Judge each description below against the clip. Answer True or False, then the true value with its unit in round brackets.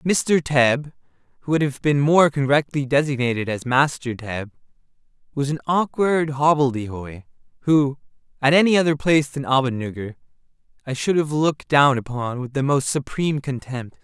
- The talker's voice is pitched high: False (140 Hz)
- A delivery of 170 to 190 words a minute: False (135 wpm)